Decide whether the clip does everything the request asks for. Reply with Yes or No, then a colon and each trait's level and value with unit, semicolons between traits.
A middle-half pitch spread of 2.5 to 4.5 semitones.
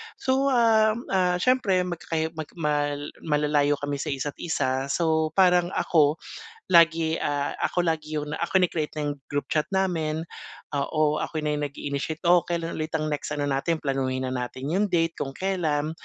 Yes: average, 3.3 semitones